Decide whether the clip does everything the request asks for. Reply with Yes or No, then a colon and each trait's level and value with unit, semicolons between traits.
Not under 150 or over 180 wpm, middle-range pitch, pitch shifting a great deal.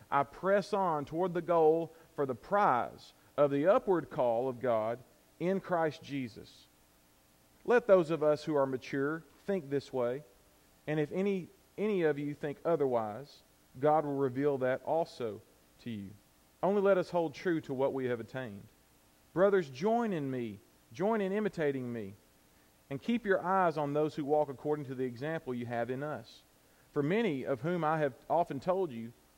Yes: average, 175 wpm; medium, 145 Hz; wide, 6.3 semitones